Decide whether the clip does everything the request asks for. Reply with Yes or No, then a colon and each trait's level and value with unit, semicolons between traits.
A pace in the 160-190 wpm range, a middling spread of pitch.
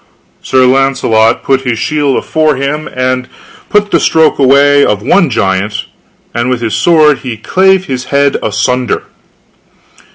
No: average, 150 wpm; average, 3.8 semitones